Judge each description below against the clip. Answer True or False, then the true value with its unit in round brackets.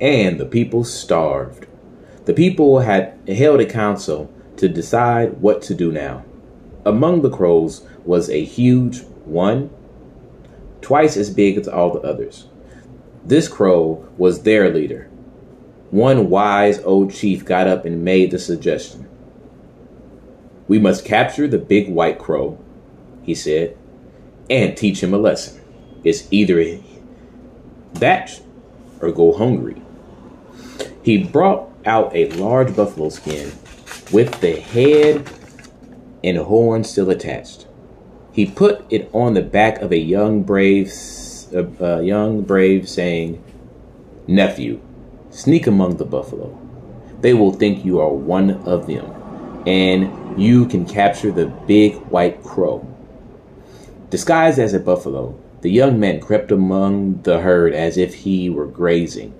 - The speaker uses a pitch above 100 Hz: False (95 Hz)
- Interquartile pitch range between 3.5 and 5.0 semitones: True (3.8 semitones)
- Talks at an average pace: False (130 wpm)